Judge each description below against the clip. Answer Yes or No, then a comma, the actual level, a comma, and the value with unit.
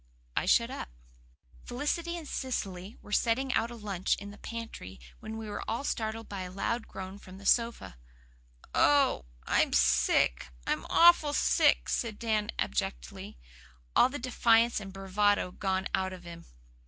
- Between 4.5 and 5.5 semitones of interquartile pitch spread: No, average, 4.0 semitones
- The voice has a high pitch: Yes, high, 210 Hz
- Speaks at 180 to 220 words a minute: No, average, 155 wpm